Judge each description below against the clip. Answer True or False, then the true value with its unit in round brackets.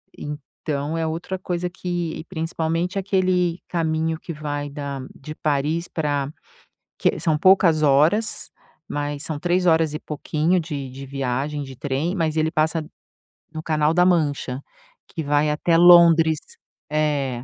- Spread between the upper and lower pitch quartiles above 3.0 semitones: False (2.7 semitones)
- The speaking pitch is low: False (155 Hz)